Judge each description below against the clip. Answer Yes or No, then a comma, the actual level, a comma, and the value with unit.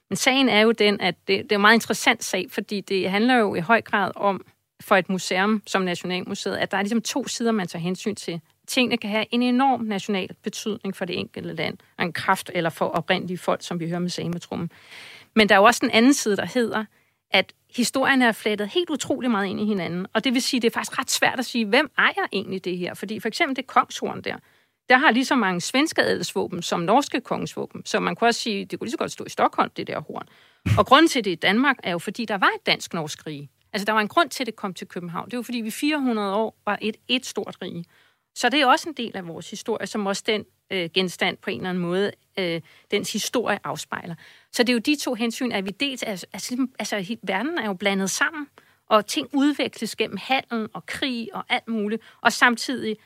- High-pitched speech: Yes, high, 215 Hz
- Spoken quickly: Yes, fast, 245 wpm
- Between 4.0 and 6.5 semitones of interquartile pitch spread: Yes, average, 4.3 semitones